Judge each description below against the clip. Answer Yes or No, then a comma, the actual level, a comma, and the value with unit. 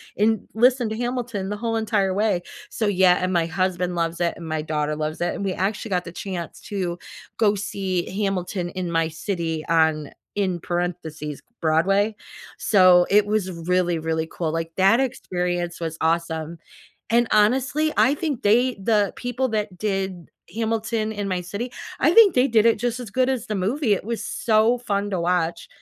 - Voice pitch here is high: Yes, high, 195 Hz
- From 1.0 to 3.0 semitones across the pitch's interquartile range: No, average, 4.3 semitones